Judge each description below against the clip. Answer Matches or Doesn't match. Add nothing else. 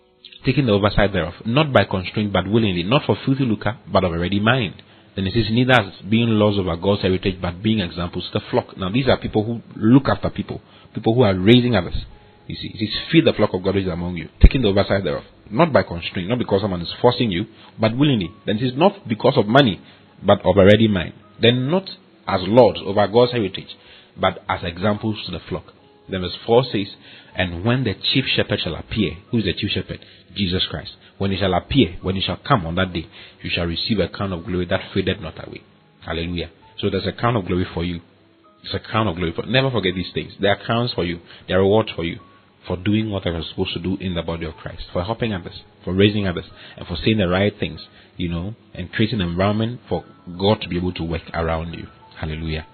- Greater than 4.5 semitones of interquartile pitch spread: Doesn't match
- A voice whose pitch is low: Matches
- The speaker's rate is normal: Doesn't match